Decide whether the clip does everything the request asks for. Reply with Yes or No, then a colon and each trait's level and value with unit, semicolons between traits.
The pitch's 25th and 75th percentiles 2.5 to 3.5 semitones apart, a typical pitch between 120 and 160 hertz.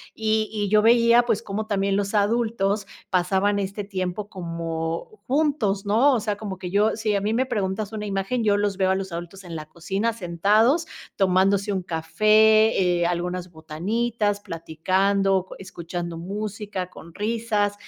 No: average, 2.9 semitones; high, 200 Hz